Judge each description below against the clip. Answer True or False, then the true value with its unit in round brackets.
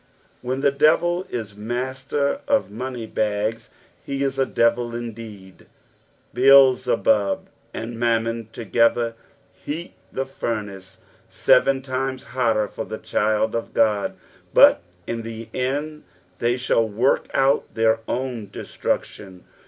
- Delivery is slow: True (120 wpm)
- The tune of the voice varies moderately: True (3.1 semitones)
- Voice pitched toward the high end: False (120 Hz)